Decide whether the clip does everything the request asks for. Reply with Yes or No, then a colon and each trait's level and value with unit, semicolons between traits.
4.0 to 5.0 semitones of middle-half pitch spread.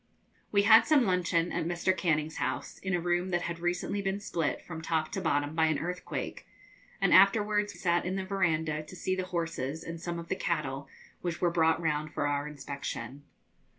No: average, 3.0 semitones